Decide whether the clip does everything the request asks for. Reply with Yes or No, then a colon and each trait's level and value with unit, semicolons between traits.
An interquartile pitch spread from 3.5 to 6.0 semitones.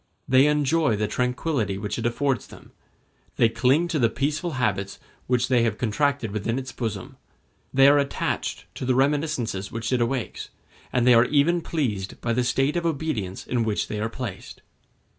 Yes: average, 4.0 semitones